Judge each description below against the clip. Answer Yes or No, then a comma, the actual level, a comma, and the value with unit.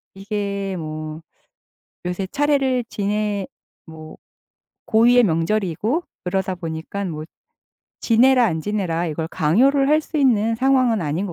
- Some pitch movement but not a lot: No, wide, 6.7 semitones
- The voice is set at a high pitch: Yes, high, 200 Hz